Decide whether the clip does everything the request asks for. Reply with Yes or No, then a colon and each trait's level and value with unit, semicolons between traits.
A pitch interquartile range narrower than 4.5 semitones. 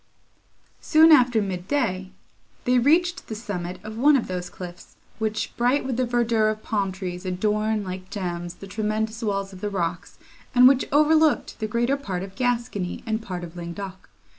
No: average, 4.8 semitones